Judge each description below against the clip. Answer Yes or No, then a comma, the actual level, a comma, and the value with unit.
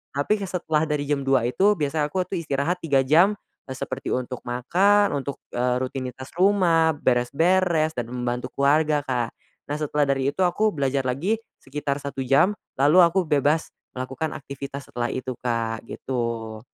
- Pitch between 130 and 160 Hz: Yes, medium, 140 Hz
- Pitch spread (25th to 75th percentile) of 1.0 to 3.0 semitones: No, average, 4.1 semitones